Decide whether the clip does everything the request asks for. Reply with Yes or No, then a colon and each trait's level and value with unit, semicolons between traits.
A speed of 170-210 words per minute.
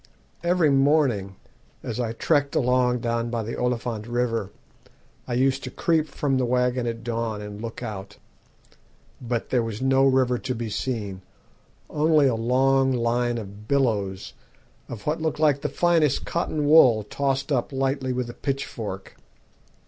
No: average, 155 wpm